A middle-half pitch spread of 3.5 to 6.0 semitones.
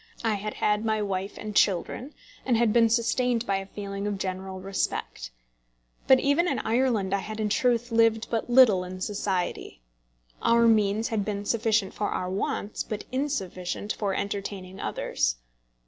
No: average, 2.9 semitones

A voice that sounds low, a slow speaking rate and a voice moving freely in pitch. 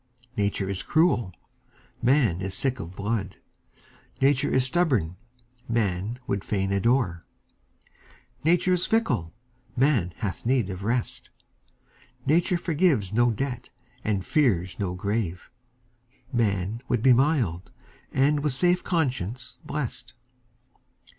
Yes: low, 120 Hz; slow, 115 wpm; wide, 6.3 semitones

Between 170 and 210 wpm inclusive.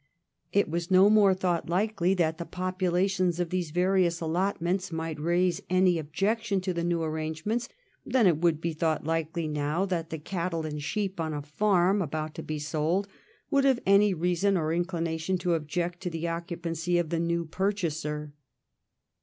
Yes: average, 180 wpm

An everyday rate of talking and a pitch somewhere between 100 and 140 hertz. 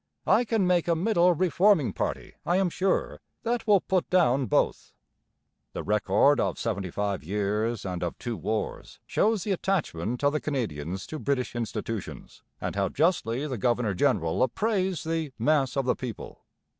Yes: average, 165 wpm; low, 135 Hz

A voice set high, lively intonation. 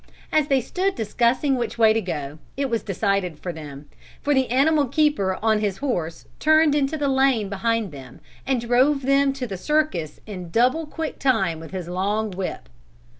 Yes: high, 230 Hz; wide, 6.6 semitones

